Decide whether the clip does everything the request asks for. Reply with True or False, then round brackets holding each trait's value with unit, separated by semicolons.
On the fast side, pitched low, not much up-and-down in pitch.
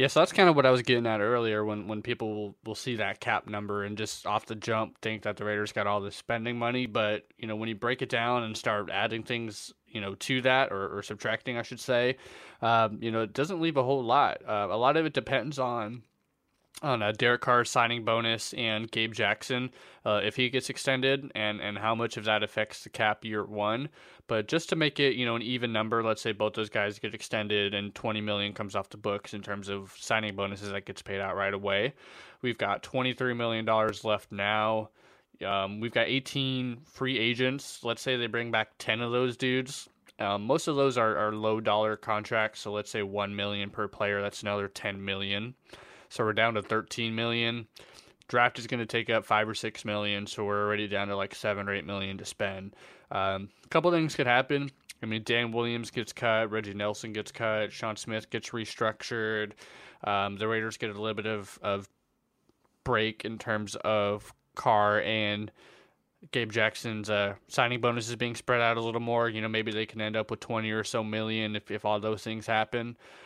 True (220 wpm; 110 Hz; 2.3 semitones)